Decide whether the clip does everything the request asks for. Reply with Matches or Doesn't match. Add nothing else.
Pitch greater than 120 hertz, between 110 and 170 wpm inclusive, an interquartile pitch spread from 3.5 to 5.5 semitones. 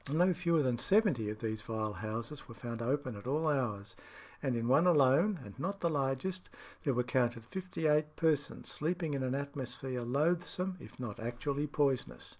Doesn't match